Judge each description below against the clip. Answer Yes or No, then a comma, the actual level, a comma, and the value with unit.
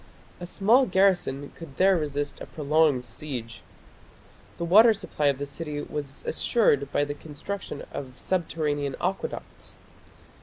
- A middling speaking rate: No, slow, 130 wpm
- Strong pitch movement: No, average, 4.4 semitones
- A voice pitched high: No, medium, 150 Hz